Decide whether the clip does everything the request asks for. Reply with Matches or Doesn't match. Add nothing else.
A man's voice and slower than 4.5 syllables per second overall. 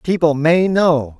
Matches